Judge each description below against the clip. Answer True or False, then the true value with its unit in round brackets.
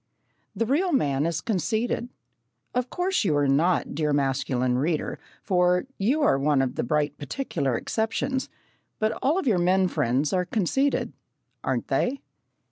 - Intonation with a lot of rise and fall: True (8.9 semitones)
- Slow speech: False (150 wpm)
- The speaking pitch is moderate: True (180 Hz)